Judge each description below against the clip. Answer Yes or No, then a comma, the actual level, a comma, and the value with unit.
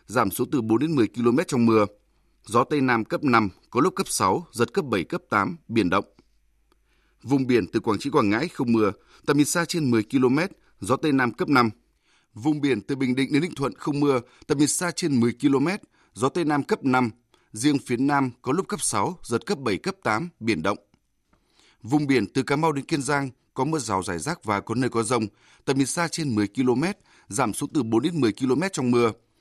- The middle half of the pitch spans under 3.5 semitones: No, average, 4.5 semitones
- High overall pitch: No, low, 130 Hz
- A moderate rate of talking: Yes, average, 230 wpm